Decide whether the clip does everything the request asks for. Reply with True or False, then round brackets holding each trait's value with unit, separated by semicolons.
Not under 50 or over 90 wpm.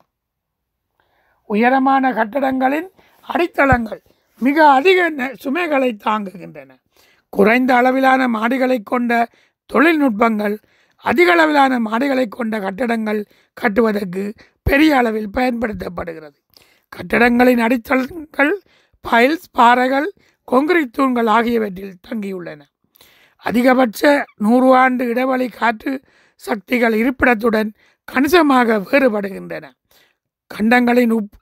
True (75 wpm)